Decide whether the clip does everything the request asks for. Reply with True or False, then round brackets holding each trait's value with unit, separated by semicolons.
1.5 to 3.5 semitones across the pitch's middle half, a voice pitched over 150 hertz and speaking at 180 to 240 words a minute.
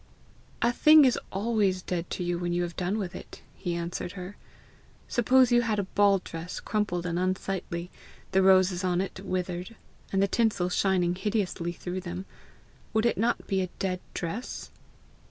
False (2.8 semitones; 185 Hz; 170 wpm)